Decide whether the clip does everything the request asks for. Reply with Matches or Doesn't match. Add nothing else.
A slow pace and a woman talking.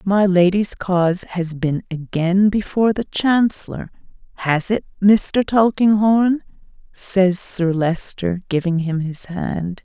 Matches